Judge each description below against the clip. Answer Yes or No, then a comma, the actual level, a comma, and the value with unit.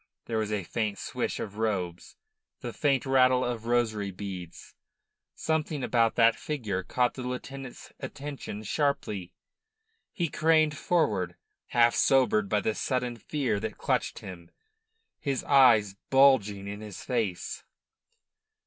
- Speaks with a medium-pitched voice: No, low, 115 Hz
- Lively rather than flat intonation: No, average, 4.6 semitones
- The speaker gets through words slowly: Yes, slow, 130 wpm